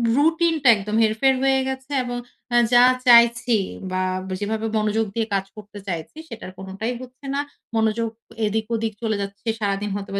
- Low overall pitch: No, high, 220 Hz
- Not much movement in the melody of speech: No, average, 3.1 semitones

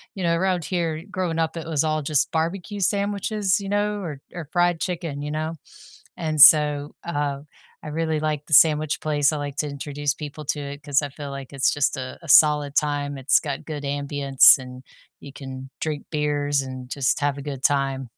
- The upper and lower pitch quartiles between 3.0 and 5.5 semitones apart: No, narrow, 2.5 semitones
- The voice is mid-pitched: Yes, medium, 150 Hz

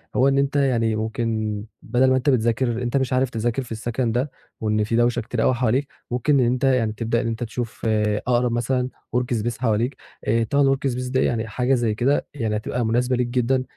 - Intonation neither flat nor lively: No, narrow, 2.2 semitones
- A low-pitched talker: Yes, low, 120 Hz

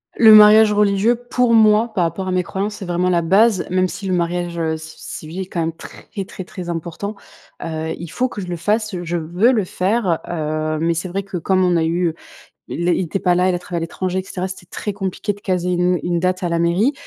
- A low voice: No, medium, 180 Hz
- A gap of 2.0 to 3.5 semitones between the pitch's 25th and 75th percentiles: Yes, average, 2.9 semitones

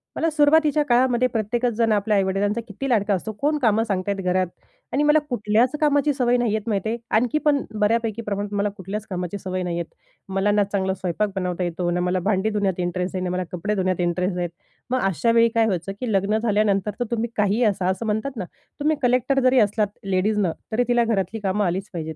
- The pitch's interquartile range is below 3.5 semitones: No, average, 3.9 semitones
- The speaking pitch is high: Yes, high, 210 Hz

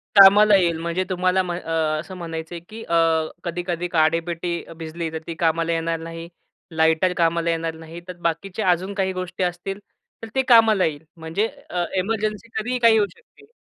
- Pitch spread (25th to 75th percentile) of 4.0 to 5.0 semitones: No, average, 3.0 semitones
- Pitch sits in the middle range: Yes, medium, 175 Hz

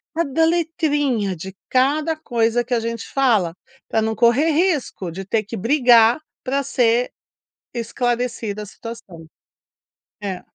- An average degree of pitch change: Yes, average, 4.1 semitones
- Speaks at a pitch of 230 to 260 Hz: Yes, high, 235 Hz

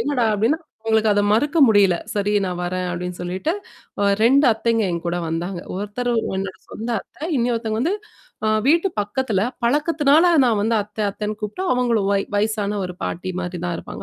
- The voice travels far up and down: No, average, 4.3 semitones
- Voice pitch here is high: Yes, high, 215 Hz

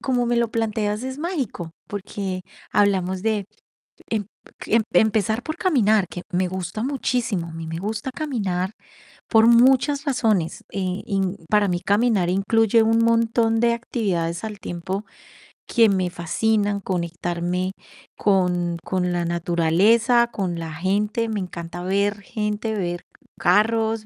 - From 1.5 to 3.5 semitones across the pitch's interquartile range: No, average, 4.0 semitones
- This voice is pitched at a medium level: No, high, 205 Hz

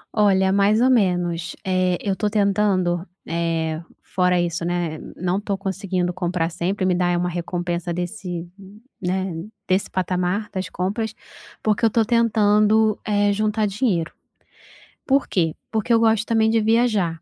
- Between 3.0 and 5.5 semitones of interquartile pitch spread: Yes, average, 3.3 semitones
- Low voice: No, high, 190 Hz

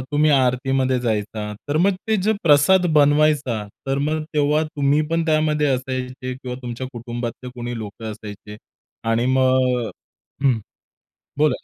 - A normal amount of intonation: Yes, average, 3.7 semitones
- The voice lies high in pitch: No, low, 130 Hz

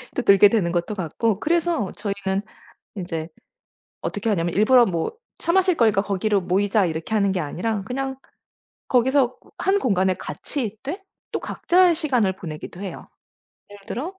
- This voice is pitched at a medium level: No, high, 205 Hz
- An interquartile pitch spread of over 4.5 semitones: Yes, wide, 5.4 semitones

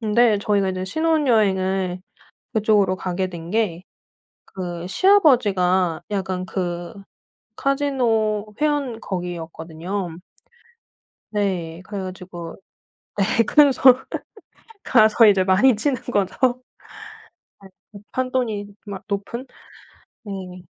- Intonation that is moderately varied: Yes, average, 4.1 semitones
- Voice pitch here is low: No, high, 200 Hz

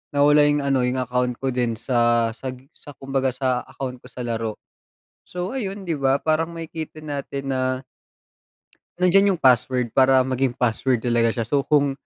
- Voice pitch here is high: No, low, 130 Hz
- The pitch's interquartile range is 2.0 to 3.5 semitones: Yes, average, 2.9 semitones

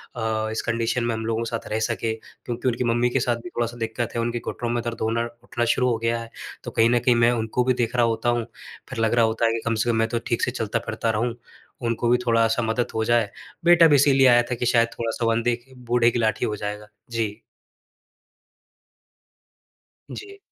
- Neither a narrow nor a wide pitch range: No, narrow, 1.2 semitones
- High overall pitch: No, low, 115 Hz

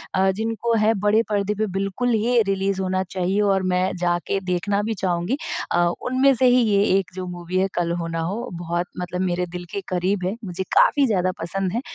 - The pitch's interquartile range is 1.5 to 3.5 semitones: Yes, average, 2.8 semitones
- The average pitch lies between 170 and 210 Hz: Yes, high, 190 Hz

